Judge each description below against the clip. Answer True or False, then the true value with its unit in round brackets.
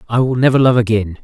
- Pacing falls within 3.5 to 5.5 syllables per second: False (6.8 syllables/s)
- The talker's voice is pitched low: True (120 Hz)